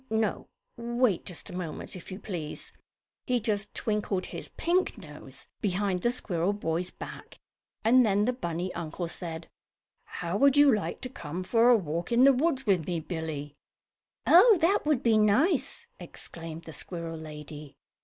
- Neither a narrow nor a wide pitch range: No, wide, 6.3 semitones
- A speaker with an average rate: Yes, average, 165 wpm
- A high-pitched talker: Yes, high, 195 Hz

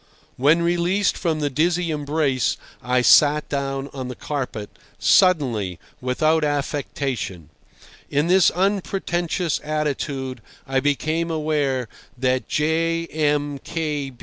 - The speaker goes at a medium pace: No, slow, 100 wpm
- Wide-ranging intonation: No, average, 3.7 semitones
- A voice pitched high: No, medium, 150 Hz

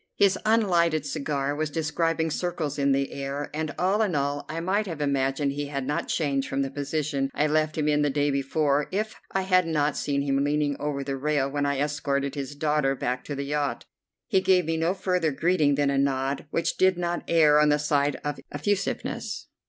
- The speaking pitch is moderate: Yes, medium, 150 Hz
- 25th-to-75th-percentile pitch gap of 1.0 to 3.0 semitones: Yes, narrow, 2.6 semitones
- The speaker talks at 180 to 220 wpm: Yes, fast, 205 wpm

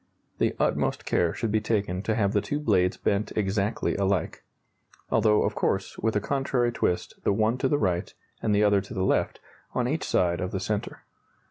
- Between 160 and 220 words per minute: Yes, average, 200 wpm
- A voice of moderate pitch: No, low, 105 Hz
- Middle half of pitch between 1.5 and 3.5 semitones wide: Yes, average, 2.7 semitones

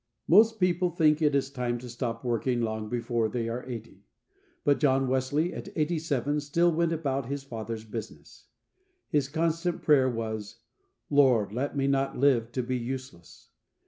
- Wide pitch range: No, average, 4.2 semitones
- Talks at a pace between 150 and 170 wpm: Yes, average, 165 wpm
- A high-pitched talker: No, low, 130 Hz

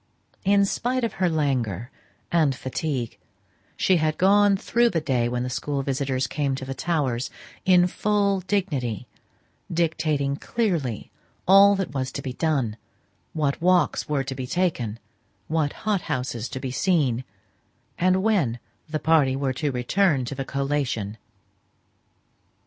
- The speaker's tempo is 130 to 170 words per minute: Yes, average, 140 wpm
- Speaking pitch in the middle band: Yes, medium, 145 Hz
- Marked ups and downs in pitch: Yes, wide, 5.9 semitones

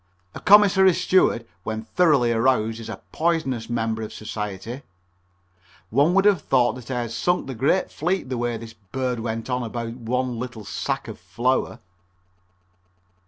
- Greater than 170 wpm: No, average, 160 wpm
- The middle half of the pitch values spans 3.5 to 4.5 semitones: Yes, average, 4.0 semitones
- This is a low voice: Yes, low, 120 Hz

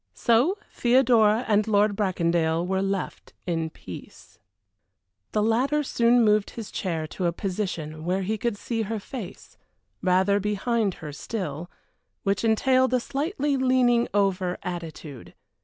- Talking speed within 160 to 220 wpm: No, slow, 135 wpm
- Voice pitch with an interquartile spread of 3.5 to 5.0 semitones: Yes, average, 4.6 semitones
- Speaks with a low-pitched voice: No, high, 205 Hz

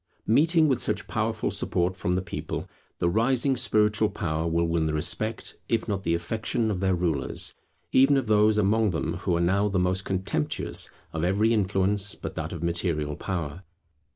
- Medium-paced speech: Yes, average, 180 wpm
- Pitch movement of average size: Yes, average, 4.2 semitones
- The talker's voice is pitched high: No, very low, 95 Hz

